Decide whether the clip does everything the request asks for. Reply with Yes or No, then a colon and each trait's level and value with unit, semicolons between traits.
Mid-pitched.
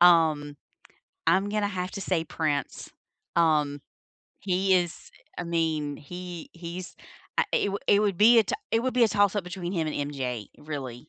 Yes: medium, 175 Hz